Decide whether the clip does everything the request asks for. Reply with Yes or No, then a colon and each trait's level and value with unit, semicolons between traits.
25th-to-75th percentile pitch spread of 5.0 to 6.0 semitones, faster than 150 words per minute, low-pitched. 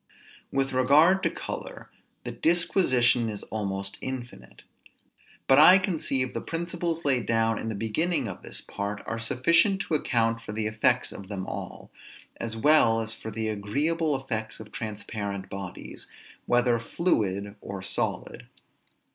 No: wide, 5.5 semitones; average, 145 wpm; low, 115 Hz